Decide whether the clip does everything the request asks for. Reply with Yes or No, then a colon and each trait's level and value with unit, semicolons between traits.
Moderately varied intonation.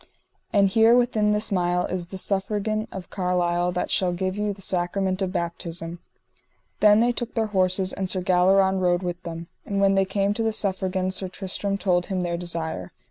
No: narrow, 2.1 semitones